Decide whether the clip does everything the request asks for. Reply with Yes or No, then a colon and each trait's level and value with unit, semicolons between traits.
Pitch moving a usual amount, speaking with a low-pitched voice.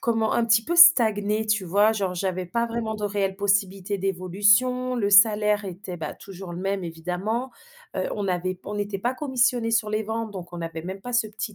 No: average, 3.1 semitones; high, 205 Hz